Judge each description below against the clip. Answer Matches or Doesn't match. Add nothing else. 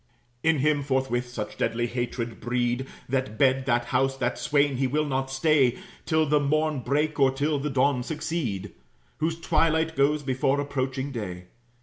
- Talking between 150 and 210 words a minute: Matches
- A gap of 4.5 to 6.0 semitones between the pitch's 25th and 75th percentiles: Doesn't match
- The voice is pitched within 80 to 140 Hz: Matches